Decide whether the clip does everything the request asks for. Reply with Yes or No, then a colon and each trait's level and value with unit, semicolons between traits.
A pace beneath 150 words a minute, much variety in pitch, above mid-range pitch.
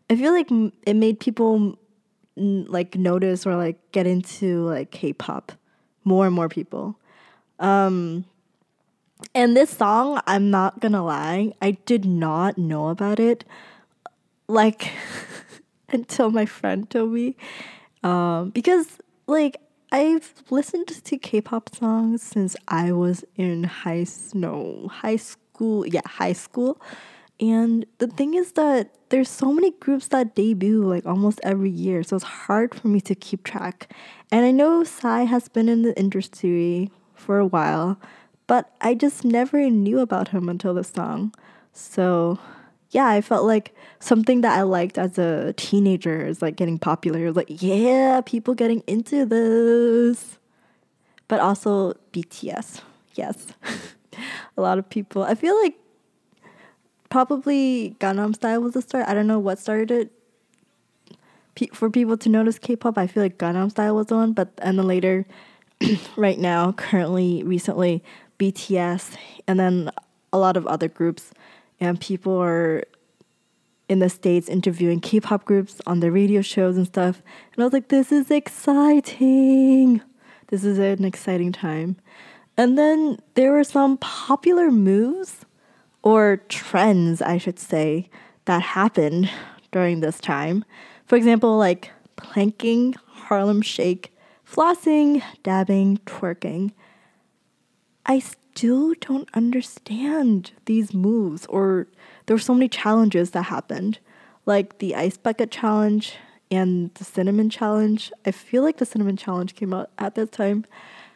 No: average, 140 wpm; average, 4.3 semitones; high, 210 Hz